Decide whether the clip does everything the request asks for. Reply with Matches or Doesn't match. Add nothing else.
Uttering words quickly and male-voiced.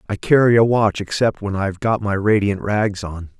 Matches